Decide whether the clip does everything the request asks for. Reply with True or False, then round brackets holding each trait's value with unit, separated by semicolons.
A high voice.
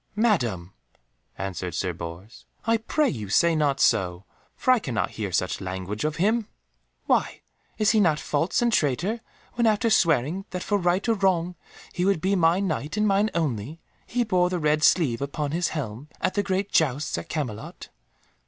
False (165 Hz)